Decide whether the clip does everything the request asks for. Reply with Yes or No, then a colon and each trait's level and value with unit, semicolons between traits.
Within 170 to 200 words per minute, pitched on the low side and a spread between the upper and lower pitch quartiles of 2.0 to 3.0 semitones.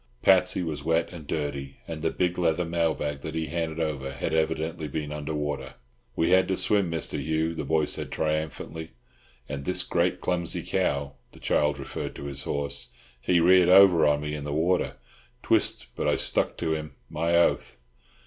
Yes: average, 185 wpm; very low, 80 Hz; narrow, 2.5 semitones